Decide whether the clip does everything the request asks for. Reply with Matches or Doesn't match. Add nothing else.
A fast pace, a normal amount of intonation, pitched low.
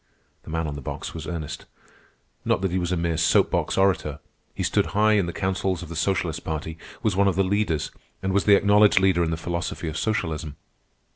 Matches